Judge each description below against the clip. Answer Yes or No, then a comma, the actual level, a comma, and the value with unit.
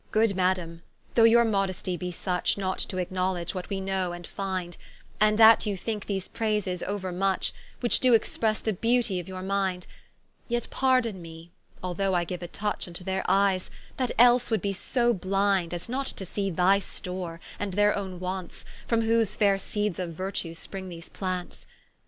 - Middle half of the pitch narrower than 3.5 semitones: Yes, average, 2.8 semitones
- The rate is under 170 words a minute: No, average, 180 wpm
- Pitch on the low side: No, high, 190 Hz